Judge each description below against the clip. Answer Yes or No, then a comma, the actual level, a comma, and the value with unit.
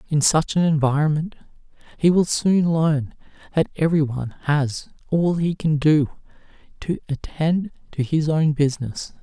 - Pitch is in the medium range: Yes, medium, 155 Hz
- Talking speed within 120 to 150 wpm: Yes, slow, 135 wpm